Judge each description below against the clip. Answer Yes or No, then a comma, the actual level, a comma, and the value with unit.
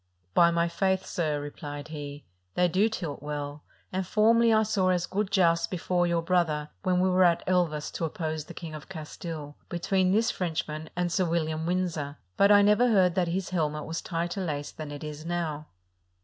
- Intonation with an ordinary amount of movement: Yes, average, 3.2 semitones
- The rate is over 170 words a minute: Yes, average, 190 wpm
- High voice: No, medium, 170 Hz